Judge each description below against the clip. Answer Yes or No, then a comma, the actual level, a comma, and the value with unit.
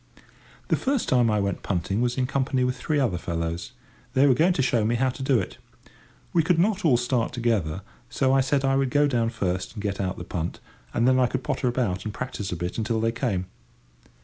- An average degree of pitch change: Yes, average, 5.0 semitones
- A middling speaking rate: No, fast, 230 wpm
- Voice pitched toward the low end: Yes, low, 120 Hz